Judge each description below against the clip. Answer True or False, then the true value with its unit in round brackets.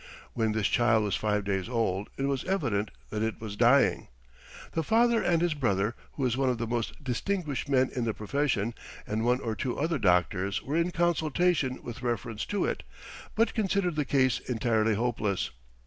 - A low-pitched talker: True (125 Hz)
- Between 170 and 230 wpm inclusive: True (185 wpm)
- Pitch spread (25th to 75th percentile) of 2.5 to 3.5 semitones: False (5.6 semitones)